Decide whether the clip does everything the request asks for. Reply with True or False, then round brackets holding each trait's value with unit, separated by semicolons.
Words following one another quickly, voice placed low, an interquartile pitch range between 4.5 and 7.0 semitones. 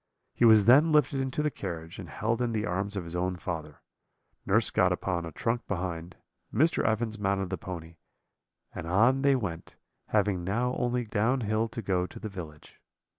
False (185 wpm; 100 Hz; 5.0 semitones)